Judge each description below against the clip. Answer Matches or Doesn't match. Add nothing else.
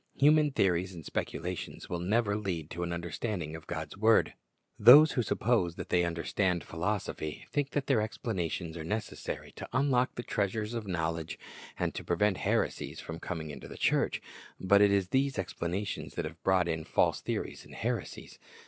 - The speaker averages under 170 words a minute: Doesn't match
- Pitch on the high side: Doesn't match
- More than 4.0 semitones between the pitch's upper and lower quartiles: Matches